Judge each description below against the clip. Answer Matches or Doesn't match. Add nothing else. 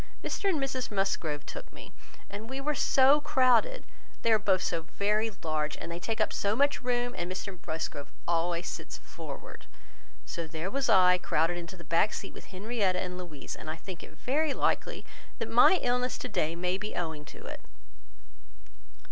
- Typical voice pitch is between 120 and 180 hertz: Doesn't match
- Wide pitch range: Matches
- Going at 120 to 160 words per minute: Doesn't match